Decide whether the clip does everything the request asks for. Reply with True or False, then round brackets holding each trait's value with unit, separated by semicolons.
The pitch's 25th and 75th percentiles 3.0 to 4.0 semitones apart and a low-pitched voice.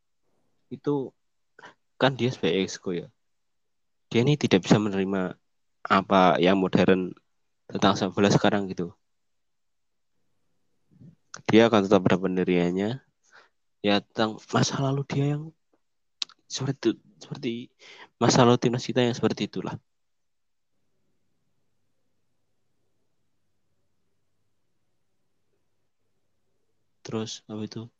False (4.7 semitones; 110 Hz)